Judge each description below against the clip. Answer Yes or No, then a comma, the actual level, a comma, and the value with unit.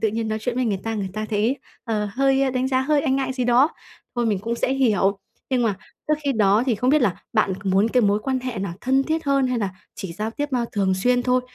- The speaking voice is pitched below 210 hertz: No, high, 240 Hz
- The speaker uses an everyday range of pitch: Yes, average, 4.0 semitones